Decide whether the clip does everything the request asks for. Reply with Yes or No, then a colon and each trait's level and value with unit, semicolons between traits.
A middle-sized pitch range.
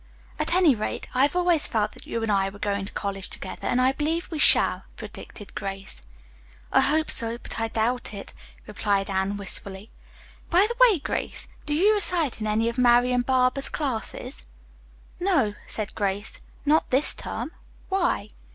No: wide, 6.7 semitones